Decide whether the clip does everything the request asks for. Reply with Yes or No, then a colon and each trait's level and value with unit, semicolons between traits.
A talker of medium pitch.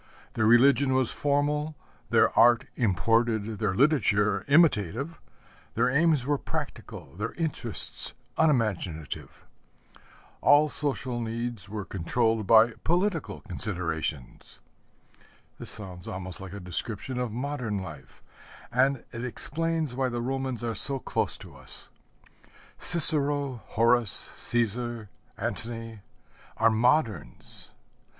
No: low, 120 Hz